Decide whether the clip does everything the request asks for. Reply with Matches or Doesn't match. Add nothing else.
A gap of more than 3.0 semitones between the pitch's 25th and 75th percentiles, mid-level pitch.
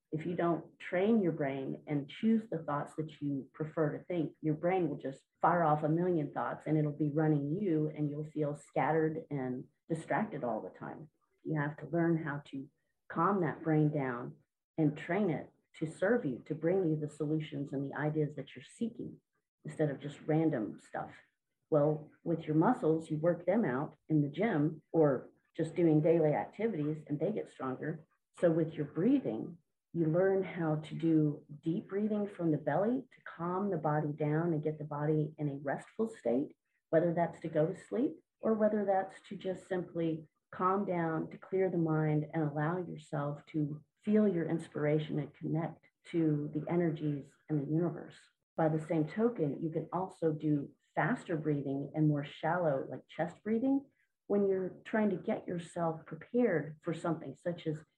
Doesn't match